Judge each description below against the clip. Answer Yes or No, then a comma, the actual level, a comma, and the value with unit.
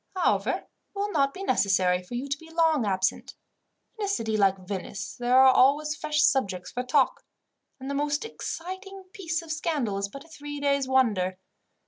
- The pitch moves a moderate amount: No, wide, 7.5 semitones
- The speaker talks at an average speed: Yes, average, 185 wpm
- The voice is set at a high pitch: Yes, very high, 275 Hz